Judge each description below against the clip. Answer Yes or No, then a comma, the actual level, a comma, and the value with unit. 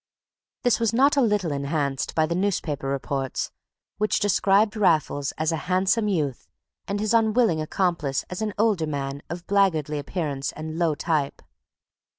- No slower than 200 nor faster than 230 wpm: No, average, 155 wpm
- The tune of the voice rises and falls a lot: Yes, wide, 5.9 semitones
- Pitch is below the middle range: No, medium, 170 Hz